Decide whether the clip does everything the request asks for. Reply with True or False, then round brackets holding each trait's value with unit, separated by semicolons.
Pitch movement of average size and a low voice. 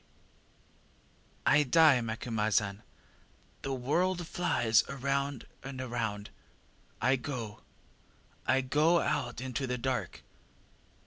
True (3.0 semitones; 130 Hz)